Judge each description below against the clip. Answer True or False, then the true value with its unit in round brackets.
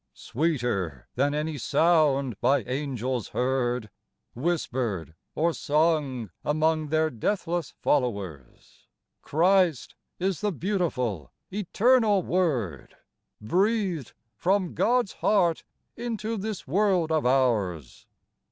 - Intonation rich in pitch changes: True (6.8 semitones)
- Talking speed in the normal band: False (95 wpm)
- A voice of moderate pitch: True (155 Hz)